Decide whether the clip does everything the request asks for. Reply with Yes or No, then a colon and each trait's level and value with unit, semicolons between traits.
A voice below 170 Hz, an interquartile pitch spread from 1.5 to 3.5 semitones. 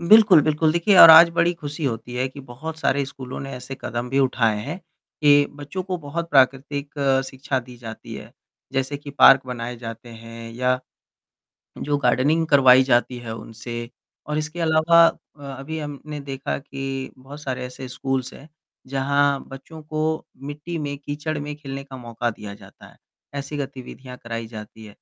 Yes: low, 135 Hz; average, 3.1 semitones